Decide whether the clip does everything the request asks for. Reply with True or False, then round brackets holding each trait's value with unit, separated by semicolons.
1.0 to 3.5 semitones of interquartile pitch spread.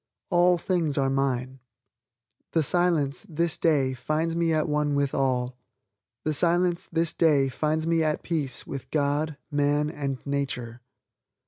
True (3.2 semitones)